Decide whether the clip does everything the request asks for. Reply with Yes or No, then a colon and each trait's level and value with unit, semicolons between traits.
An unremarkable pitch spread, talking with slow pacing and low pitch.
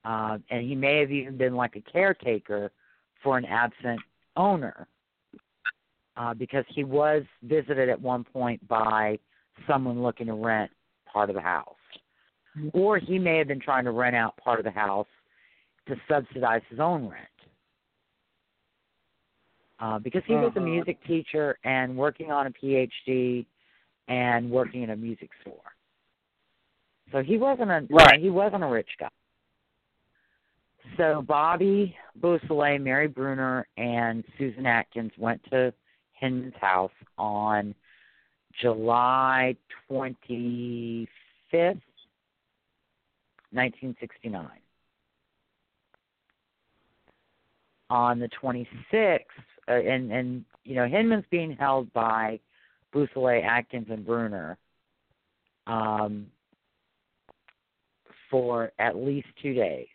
Yes: average, 4.1 semitones; slow, 115 wpm; low, 125 Hz